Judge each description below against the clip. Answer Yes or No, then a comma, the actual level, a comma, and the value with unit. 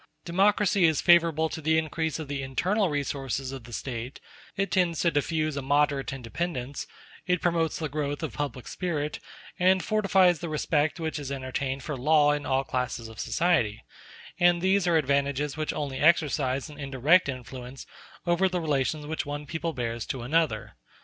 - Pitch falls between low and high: Yes, medium, 150 Hz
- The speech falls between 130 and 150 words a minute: No, average, 170 wpm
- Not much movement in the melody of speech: No, average, 3.8 semitones